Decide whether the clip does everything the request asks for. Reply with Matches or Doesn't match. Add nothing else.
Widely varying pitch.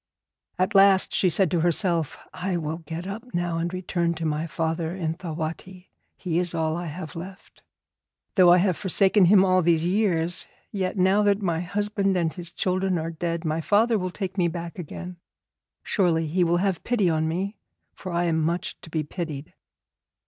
Doesn't match